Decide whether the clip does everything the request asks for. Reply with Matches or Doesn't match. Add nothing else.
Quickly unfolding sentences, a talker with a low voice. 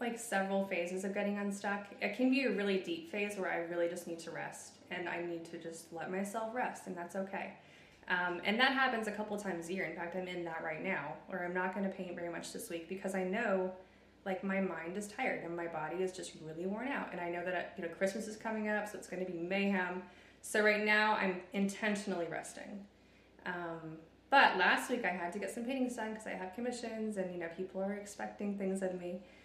Doesn't match